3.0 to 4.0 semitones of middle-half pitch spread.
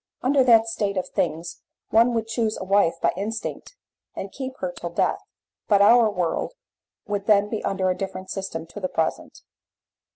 Yes: average, 3.3 semitones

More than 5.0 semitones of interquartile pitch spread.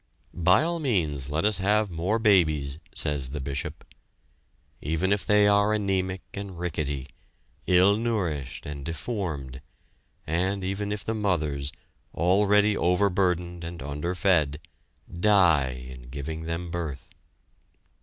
Yes: wide, 5.4 semitones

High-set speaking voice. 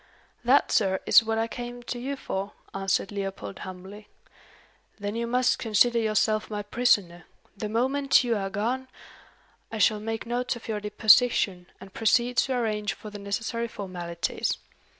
Yes: high, 215 Hz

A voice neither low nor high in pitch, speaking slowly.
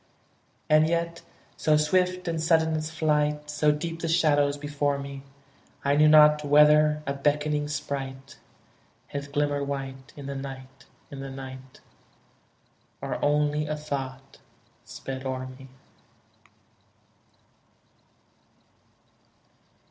Yes: medium, 145 Hz; slow, 110 wpm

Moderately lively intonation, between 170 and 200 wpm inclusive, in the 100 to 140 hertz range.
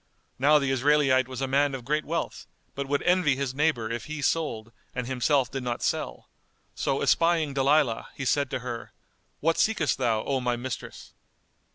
Yes: average, 3.1 semitones; average, 180 wpm; low, 135 Hz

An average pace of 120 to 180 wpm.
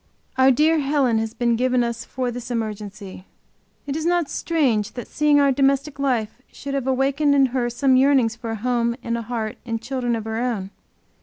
No: average, 200 wpm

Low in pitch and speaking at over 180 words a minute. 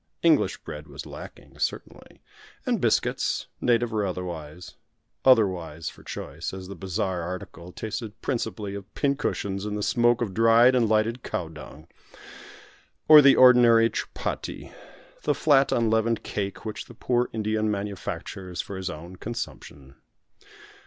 No: low, 105 Hz; average, 140 wpm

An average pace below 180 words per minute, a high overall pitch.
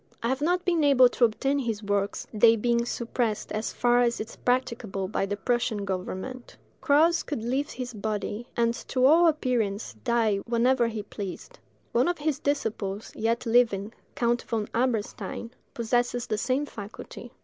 Yes: average, 160 wpm; high, 235 Hz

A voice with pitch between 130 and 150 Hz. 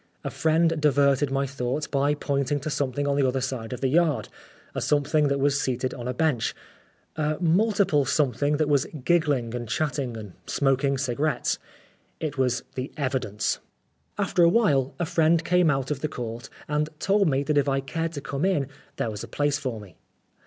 Yes: medium, 140 Hz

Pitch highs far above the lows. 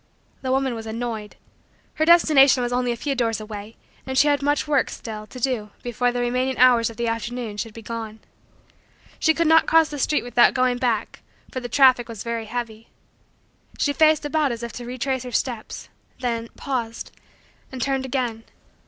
No: average, 2.7 semitones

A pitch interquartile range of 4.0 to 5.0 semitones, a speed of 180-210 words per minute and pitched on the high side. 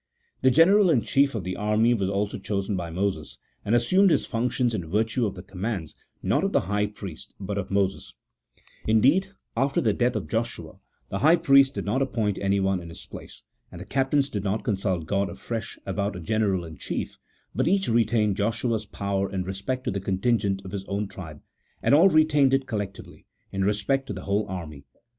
No: average, 4.3 semitones; average, 200 wpm; low, 105 Hz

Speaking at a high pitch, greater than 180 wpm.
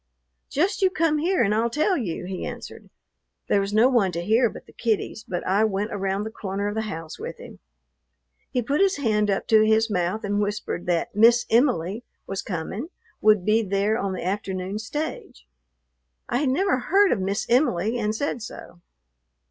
Yes: high, 215 Hz; average, 190 wpm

